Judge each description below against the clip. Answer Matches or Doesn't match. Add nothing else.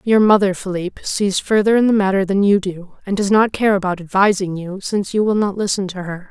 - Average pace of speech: Doesn't match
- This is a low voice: Doesn't match